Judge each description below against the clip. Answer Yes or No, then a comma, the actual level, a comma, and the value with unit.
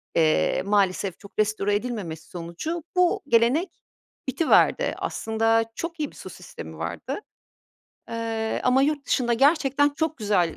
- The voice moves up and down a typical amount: No, wide, 6.0 semitones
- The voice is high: Yes, high, 230 Hz